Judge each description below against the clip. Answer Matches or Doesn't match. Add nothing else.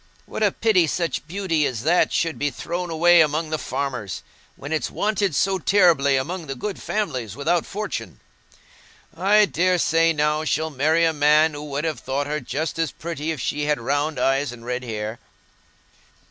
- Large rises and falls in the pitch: Doesn't match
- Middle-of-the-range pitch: Matches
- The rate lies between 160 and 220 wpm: Matches